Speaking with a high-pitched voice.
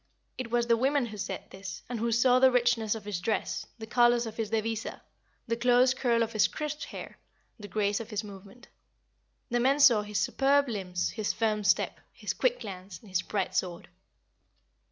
Yes: high, 225 Hz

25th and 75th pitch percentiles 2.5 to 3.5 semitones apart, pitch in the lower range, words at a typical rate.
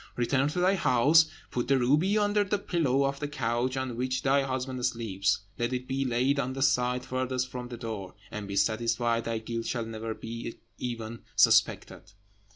Yes: average, 2.8 semitones; low, 125 Hz; average, 185 wpm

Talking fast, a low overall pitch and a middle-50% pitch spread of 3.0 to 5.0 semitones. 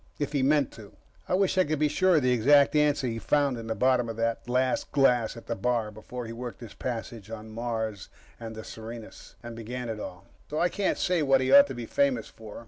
Yes: fast, 240 wpm; low, 125 Hz; average, 4.0 semitones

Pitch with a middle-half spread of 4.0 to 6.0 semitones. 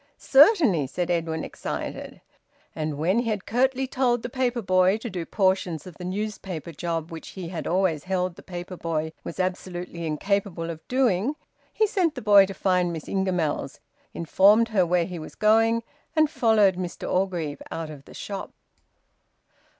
Yes: average, 4.6 semitones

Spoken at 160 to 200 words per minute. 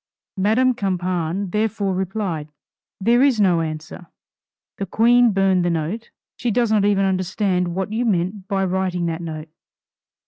No: average, 145 wpm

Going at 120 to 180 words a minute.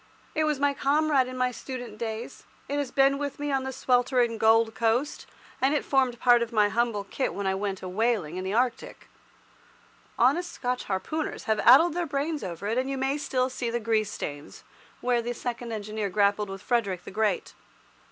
No: average, 200 wpm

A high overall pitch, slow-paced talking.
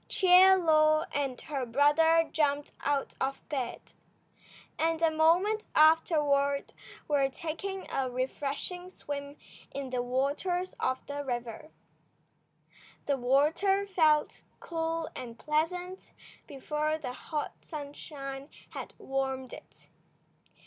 Yes: very high, 295 Hz; slow, 105 wpm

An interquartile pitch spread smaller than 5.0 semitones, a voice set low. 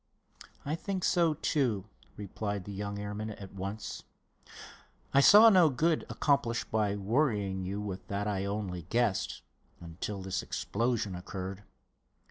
Yes: average, 4.4 semitones; low, 105 Hz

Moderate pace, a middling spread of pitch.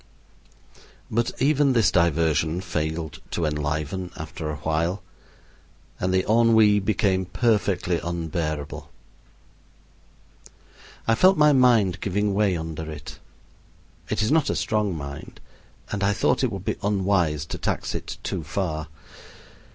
No: slow, 125 wpm; average, 5.0 semitones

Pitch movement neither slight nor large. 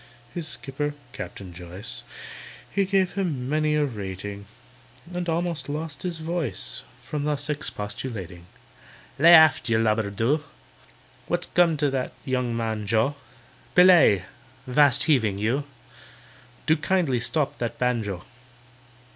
No: wide, 6.4 semitones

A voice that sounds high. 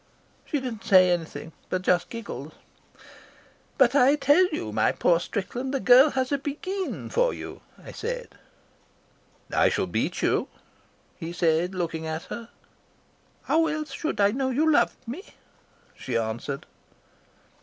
Yes: high, 230 Hz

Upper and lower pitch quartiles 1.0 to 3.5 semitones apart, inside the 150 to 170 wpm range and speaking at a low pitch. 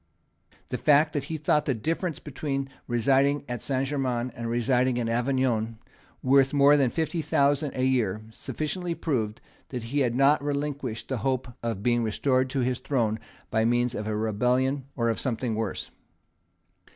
Yes: average, 3.2 semitones; average, 165 wpm; low, 130 Hz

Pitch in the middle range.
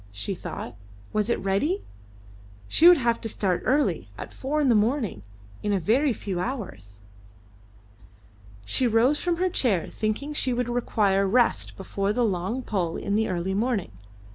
No: high, 220 Hz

